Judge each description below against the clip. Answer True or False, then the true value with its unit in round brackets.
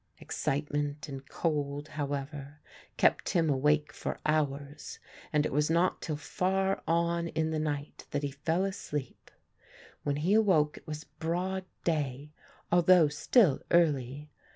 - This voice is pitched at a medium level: True (150 Hz)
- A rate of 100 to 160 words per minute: True (135 wpm)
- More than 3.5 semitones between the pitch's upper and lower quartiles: False (2.7 semitones)